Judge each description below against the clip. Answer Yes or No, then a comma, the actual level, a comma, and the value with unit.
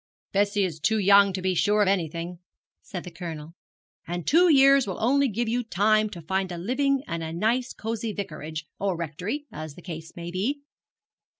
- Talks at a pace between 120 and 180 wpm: No, average, 190 wpm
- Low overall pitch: No, high, 195 Hz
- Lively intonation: No, average, 4.9 semitones